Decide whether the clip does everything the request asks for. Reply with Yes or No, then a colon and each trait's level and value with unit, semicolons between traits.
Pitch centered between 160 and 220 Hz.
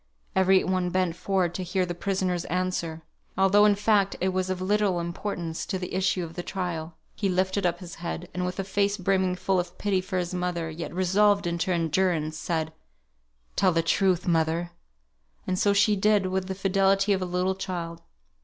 Yes: medium, 185 Hz